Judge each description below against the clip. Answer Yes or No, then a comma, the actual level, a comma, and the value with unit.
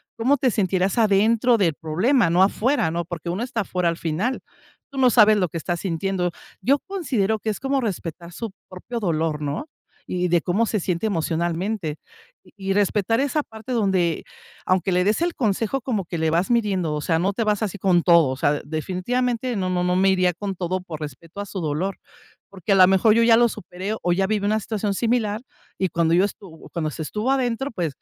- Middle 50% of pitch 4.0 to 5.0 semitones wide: Yes, average, 4.5 semitones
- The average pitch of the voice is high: Yes, high, 195 Hz